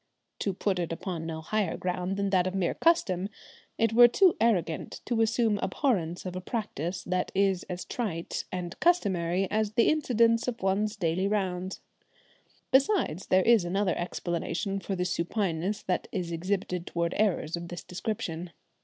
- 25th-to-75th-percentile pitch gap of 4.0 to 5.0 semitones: No, average, 3.5 semitones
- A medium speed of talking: Yes, average, 160 wpm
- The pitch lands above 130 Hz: Yes, high, 190 Hz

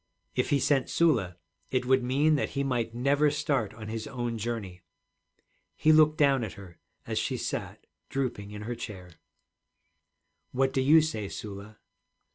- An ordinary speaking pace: Yes, average, 160 wpm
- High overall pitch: No, low, 125 Hz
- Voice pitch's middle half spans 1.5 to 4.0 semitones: No, average, 4.8 semitones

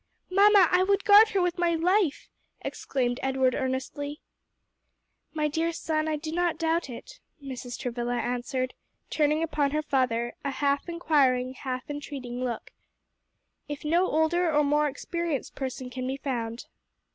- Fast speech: No, average, 145 wpm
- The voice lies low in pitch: No, very high, 290 Hz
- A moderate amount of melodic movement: Yes, average, 4.4 semitones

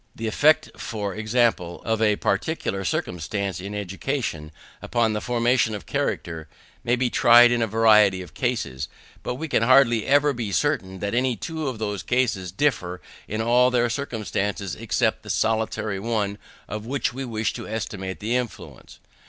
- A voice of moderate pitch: No, low, 110 Hz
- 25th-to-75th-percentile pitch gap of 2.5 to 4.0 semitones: Yes, average, 3.6 semitones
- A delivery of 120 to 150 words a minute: No, average, 165 wpm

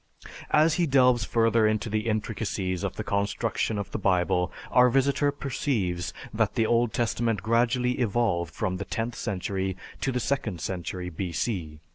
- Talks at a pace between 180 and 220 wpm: No, average, 155 wpm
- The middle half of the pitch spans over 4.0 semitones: Yes, average, 4.5 semitones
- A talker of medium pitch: No, low, 110 Hz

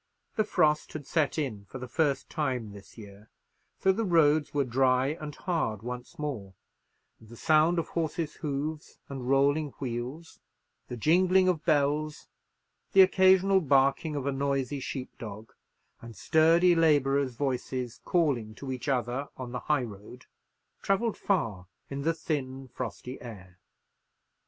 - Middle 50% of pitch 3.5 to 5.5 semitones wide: Yes, average, 4.2 semitones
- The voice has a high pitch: No, medium, 140 Hz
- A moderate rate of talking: Yes, average, 145 wpm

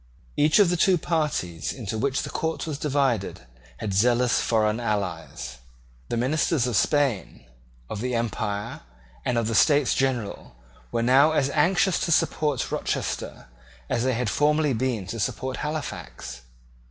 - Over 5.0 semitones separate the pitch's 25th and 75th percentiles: Yes, wide, 5.4 semitones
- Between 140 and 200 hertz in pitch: No, low, 125 Hz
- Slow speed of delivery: No, average, 150 wpm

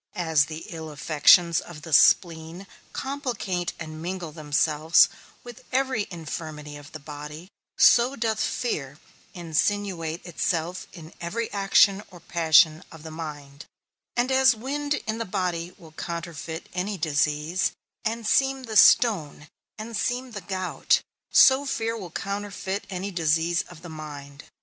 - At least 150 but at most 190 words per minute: No, average, 140 wpm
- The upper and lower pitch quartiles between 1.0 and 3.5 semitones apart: No, average, 5.1 semitones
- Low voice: No, medium, 175 Hz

